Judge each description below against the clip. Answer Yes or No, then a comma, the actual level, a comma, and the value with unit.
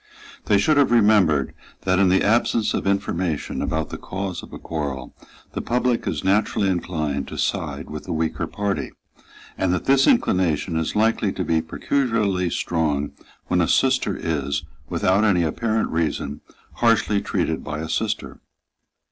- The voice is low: Yes, very low, 95 Hz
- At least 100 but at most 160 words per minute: Yes, average, 155 wpm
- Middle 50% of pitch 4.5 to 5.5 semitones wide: Yes, average, 5.1 semitones